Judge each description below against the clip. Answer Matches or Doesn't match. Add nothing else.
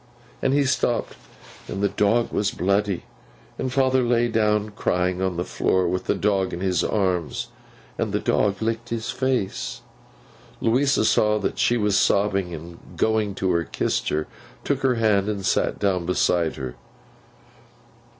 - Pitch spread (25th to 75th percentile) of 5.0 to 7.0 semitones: Doesn't match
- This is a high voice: Doesn't match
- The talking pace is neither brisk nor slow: Matches